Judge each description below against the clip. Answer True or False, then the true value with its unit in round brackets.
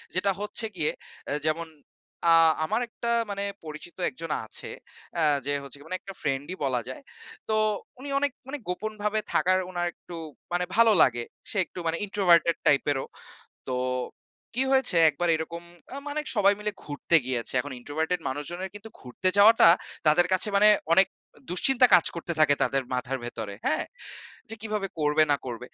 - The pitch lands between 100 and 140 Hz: False (175 Hz)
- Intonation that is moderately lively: False (6.0 semitones)